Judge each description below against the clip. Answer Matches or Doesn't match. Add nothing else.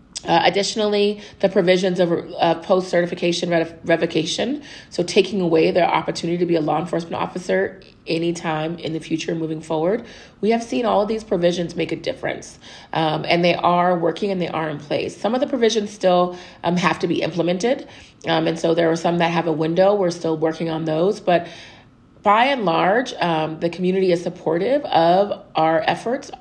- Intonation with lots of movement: Doesn't match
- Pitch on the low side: Doesn't match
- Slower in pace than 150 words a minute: Doesn't match